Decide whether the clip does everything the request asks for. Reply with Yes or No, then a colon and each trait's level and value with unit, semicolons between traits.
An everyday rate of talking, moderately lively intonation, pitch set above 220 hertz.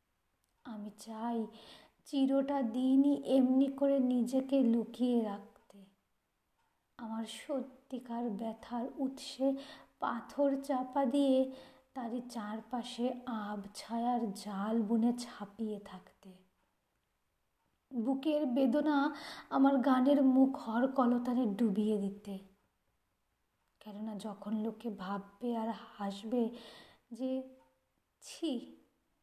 Yes: average, 80 wpm; average, 3.7 semitones; high, 240 Hz